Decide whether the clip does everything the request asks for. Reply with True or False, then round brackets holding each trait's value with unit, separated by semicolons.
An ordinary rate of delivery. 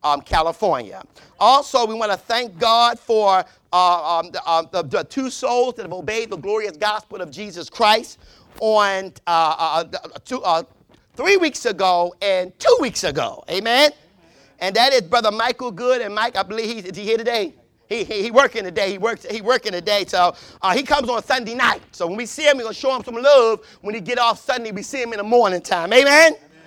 False (215 wpm)